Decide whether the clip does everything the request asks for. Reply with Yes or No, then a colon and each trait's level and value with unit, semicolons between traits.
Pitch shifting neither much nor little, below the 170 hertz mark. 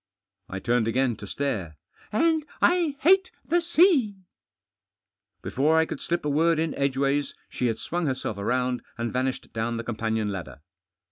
No: wide, 7.2 semitones; low, 135 Hz